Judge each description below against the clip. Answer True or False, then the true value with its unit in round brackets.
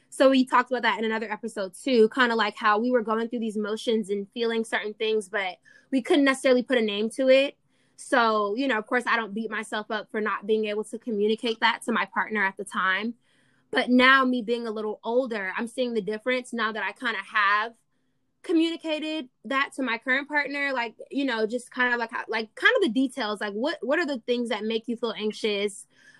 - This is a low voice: False (230 Hz)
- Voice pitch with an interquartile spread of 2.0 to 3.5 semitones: True (3.2 semitones)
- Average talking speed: False (235 wpm)